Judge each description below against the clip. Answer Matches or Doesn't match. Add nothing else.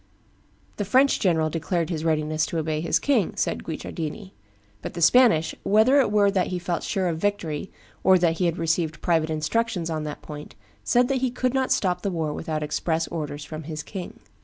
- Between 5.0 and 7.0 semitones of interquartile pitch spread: Doesn't match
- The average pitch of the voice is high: Doesn't match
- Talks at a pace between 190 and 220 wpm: Matches